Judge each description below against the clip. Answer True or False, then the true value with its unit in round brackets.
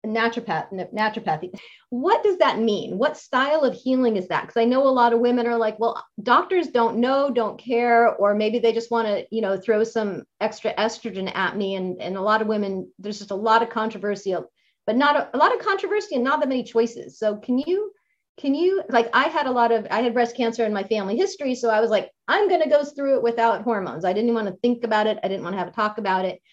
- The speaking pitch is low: False (230 Hz)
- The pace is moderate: False (255 wpm)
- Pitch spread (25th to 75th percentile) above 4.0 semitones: False (3.4 semitones)